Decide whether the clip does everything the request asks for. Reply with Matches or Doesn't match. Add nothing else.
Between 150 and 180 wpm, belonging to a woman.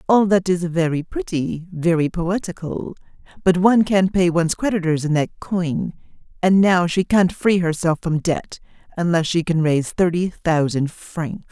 Matches